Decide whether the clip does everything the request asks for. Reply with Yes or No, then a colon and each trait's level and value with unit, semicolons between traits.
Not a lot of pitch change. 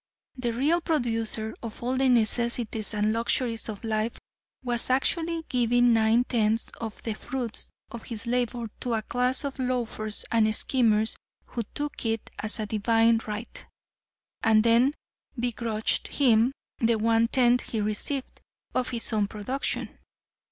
Yes: narrow, 2.3 semitones